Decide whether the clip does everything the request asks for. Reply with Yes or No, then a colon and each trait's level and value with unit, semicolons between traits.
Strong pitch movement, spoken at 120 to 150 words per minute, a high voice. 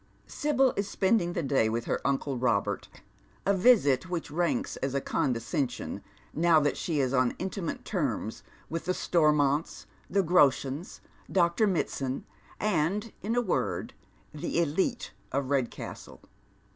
No: wide, 5.9 semitones; slow, 135 wpm; medium, 160 Hz